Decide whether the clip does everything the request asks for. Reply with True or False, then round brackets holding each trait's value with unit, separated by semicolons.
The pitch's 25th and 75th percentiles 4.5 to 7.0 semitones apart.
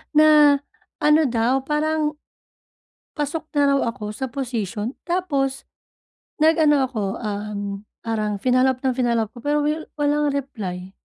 True (5.0 semitones)